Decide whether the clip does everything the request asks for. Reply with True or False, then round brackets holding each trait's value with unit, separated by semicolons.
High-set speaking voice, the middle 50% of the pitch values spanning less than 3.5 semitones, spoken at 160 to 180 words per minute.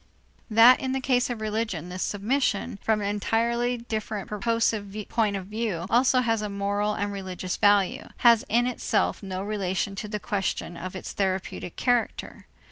True (210 Hz; 2.8 semitones; 165 wpm)